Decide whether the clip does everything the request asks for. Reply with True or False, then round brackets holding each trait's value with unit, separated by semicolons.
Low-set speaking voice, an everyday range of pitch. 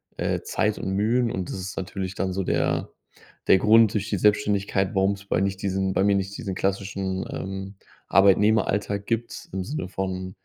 False (95 Hz; 1.3 semitones)